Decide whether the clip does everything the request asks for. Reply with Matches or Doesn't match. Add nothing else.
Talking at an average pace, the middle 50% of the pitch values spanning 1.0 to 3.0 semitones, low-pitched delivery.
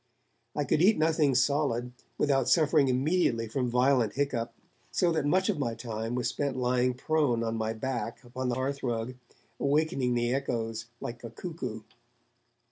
Doesn't match